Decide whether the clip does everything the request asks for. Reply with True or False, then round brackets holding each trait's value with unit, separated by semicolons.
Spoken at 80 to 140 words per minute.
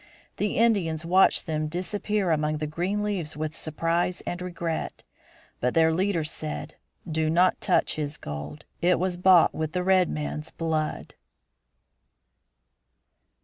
True (135 wpm)